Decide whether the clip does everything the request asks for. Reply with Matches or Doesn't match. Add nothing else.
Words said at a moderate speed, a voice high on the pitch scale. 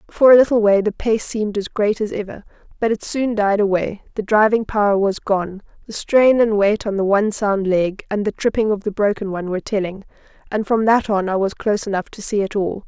Doesn't match